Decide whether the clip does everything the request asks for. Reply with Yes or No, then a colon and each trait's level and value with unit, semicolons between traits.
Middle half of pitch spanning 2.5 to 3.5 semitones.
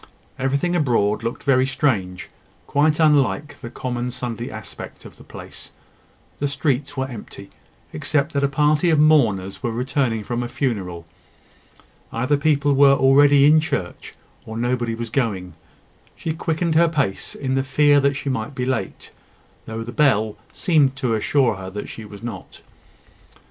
No: average, 4.2 semitones